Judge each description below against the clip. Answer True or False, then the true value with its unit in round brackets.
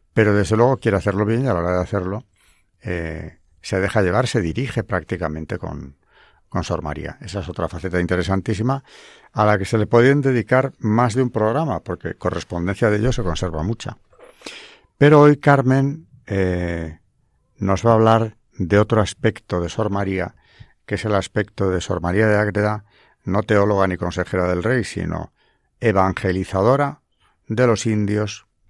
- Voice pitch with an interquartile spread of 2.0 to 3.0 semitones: False (4.2 semitones)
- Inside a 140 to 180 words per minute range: True (165 wpm)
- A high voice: False (105 Hz)